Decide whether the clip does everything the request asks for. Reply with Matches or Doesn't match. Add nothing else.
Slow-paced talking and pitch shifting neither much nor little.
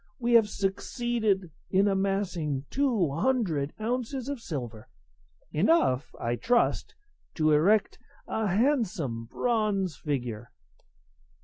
Doesn't match